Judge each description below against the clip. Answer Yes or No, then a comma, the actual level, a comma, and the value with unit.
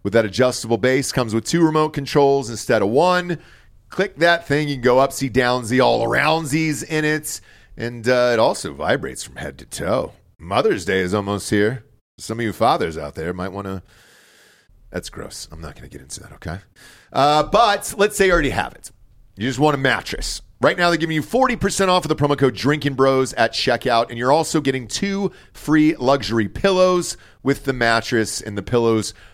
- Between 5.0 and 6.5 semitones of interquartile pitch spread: Yes, wide, 5.5 semitones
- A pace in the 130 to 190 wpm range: No, average, 200 wpm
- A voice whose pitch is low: Yes, low, 130 Hz